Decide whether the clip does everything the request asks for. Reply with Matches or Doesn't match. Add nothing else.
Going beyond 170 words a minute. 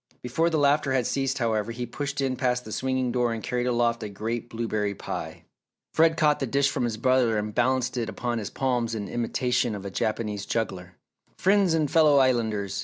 Matches